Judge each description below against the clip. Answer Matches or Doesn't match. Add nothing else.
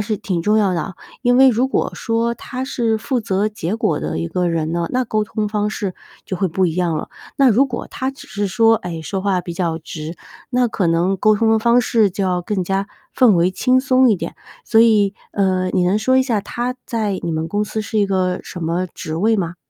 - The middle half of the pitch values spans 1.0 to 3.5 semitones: Doesn't match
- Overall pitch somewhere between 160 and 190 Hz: Doesn't match